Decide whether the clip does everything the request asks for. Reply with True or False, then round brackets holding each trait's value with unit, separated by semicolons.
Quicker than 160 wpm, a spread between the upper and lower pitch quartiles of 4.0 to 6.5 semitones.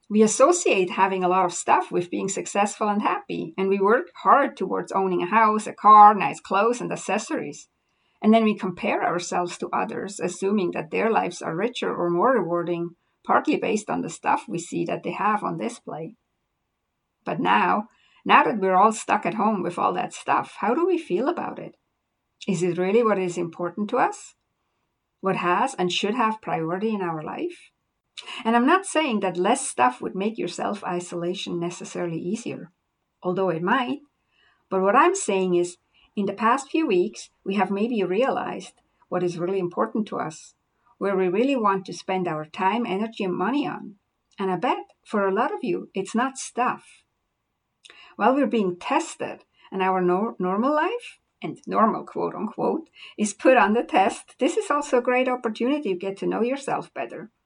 True (190 wpm; 4.8 semitones)